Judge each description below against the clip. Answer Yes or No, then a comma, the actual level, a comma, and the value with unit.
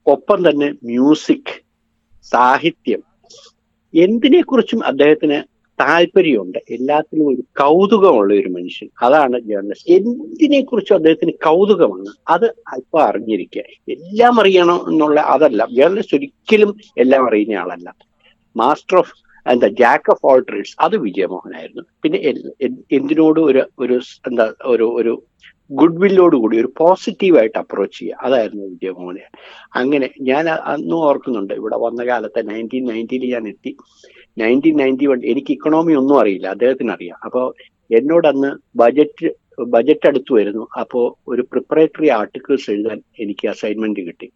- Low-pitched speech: No, medium, 145 Hz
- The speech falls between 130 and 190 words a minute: No, average, 120 wpm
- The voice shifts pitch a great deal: Yes, wide, 7.7 semitones